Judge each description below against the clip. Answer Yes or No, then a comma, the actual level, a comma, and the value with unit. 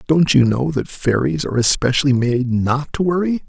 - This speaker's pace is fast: No, average, 190 wpm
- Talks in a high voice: No, low, 135 Hz